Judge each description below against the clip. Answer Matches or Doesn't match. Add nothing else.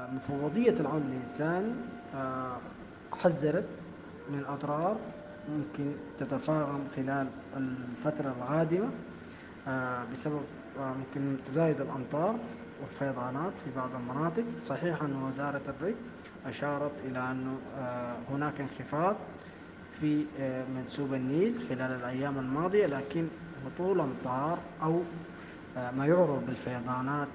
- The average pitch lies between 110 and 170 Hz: Matches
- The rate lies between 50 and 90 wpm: Doesn't match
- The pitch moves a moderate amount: Matches